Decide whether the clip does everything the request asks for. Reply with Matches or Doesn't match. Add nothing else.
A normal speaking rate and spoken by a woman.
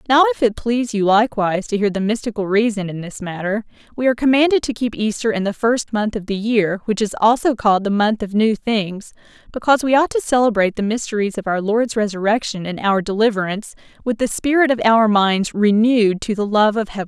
Doesn't match